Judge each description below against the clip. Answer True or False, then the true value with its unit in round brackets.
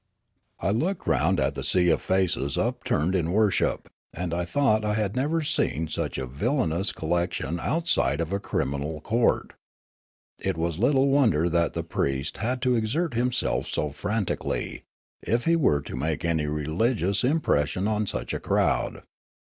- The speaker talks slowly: False (165 wpm)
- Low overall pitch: True (95 Hz)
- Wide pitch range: True (7.2 semitones)